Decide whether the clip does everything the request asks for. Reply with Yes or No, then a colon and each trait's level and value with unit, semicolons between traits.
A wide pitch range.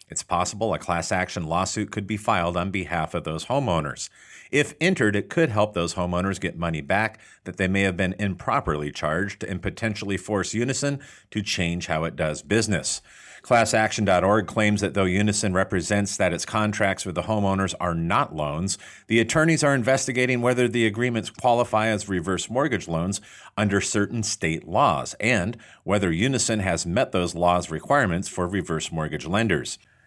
No: average, 3.8 semitones